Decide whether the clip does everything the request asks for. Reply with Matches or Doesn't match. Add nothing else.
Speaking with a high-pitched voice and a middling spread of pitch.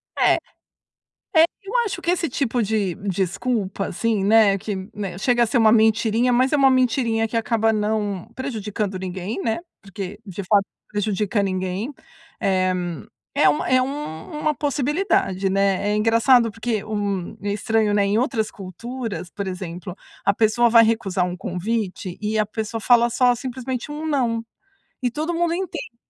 Matches